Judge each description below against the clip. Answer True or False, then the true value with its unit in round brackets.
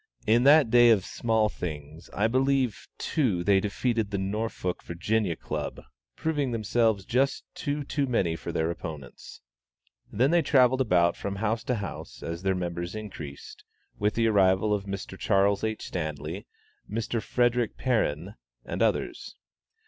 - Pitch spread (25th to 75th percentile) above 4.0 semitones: True (4.8 semitones)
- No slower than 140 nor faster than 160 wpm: True (150 wpm)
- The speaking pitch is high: False (105 Hz)